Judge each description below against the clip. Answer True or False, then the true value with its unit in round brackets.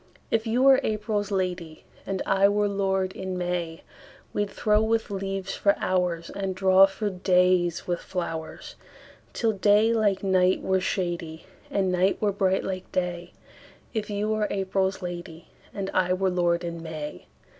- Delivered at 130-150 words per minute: True (135 wpm)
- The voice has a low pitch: False (190 Hz)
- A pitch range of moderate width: False (2.3 semitones)